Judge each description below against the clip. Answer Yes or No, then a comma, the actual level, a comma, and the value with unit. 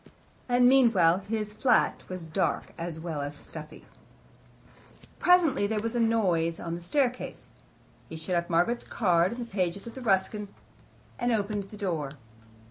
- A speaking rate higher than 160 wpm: No, average, 150 wpm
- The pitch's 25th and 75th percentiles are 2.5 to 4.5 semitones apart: No, wide, 5.4 semitones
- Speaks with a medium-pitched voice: No, high, 200 Hz